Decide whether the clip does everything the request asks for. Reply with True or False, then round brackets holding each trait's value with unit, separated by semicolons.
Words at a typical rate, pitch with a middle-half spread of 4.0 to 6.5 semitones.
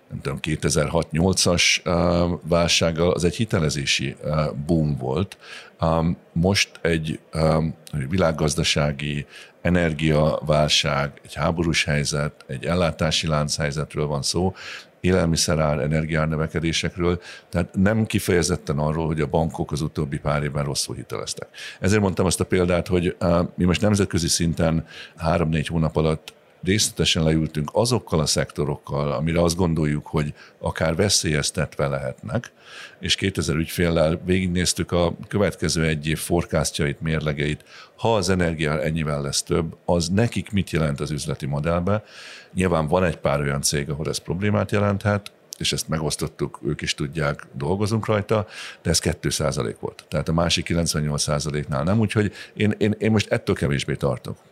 False (130 wpm; 3.1 semitones)